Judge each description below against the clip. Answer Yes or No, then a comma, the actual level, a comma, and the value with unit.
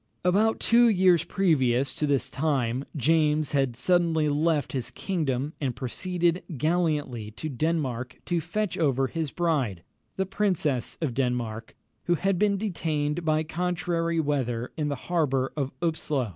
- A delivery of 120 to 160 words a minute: Yes, average, 145 wpm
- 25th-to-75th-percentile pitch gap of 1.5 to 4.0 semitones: No, average, 4.8 semitones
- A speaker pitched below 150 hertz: No, medium, 155 Hz